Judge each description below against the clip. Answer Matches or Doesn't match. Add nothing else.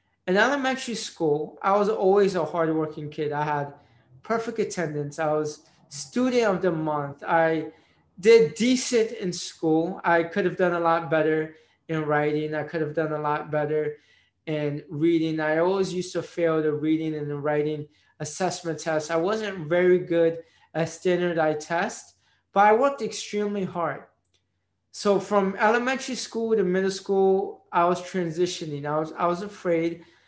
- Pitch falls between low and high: Matches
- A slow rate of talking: Doesn't match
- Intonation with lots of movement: Doesn't match